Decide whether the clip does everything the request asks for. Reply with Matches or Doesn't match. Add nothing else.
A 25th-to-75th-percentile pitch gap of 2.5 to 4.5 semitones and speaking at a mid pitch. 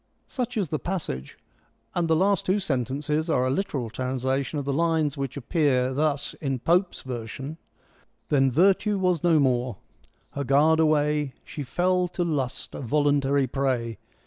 Matches